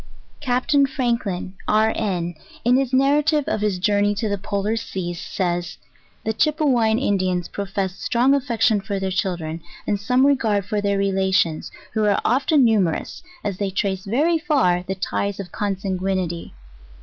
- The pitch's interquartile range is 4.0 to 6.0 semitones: Yes, average, 4.5 semitones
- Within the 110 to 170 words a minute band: Yes, average, 160 wpm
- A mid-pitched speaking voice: No, high, 205 Hz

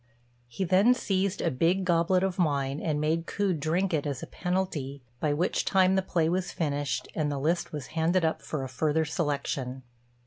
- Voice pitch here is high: No, medium, 160 Hz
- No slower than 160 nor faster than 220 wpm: Yes, average, 195 wpm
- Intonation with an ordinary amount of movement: Yes, average, 4.0 semitones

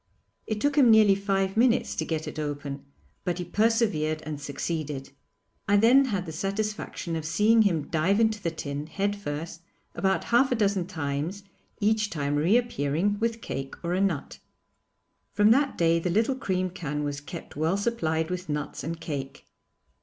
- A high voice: No, medium, 180 Hz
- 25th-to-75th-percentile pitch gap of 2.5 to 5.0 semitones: No, wide, 5.5 semitones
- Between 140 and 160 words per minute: No, average, 170 wpm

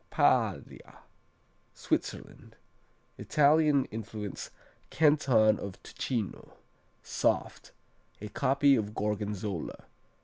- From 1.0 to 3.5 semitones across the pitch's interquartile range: No, average, 5.0 semitones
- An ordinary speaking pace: No, slow, 70 wpm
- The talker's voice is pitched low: Yes, low, 110 Hz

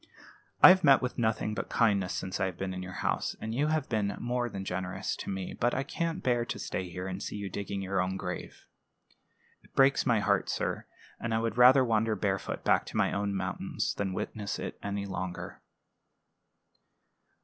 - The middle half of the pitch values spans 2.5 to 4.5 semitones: Yes, average, 4.1 semitones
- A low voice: Yes, low, 100 Hz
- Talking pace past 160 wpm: Yes, average, 195 wpm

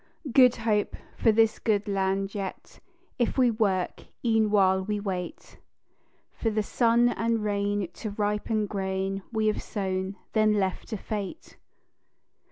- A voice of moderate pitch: No, high, 210 Hz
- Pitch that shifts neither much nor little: No, narrow, 2.3 semitones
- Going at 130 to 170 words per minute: Yes, average, 140 wpm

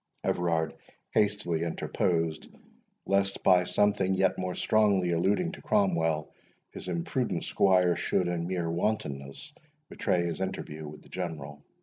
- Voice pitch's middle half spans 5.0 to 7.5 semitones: No, average, 2.9 semitones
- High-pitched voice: No, very low, 90 Hz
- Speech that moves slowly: Yes, slow, 125 wpm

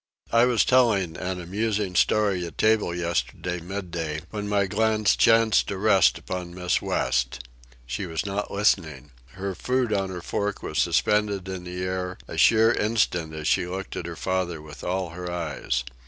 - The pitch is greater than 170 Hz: No, very low, 95 Hz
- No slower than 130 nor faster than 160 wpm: No, average, 170 wpm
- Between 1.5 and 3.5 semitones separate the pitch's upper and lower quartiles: Yes, average, 3.2 semitones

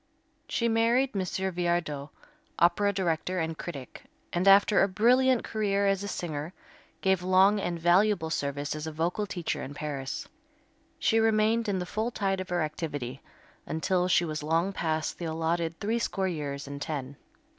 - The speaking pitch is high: No, medium, 175 Hz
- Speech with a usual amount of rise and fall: Yes, average, 4.3 semitones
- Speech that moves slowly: No, average, 160 wpm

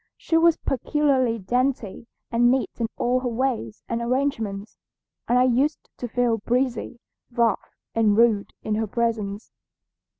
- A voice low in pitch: No, high, 235 Hz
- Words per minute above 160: No, average, 140 wpm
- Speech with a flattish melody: Yes, narrow, 2.3 semitones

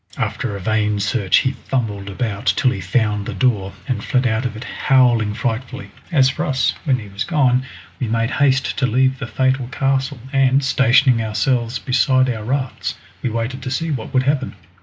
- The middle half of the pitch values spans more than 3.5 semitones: No, average, 3.2 semitones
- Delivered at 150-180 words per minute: No, average, 190 wpm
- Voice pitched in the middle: No, low, 125 Hz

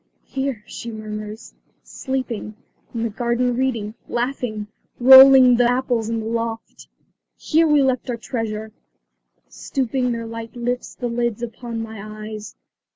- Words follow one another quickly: No, slow, 135 wpm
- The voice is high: Yes, high, 235 Hz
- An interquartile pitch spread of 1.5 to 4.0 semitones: Yes, narrow, 2.4 semitones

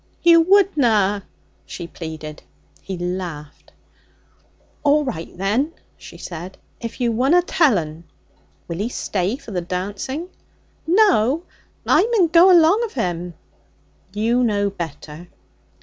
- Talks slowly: Yes, slow, 120 wpm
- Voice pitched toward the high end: Yes, high, 210 Hz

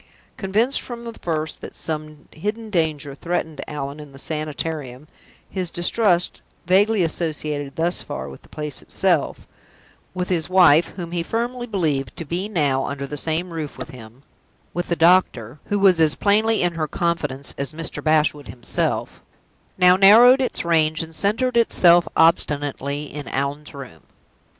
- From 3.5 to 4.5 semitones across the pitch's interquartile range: Yes, average, 4.1 semitones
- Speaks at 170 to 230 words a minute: No, average, 155 wpm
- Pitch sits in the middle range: Yes, medium, 165 Hz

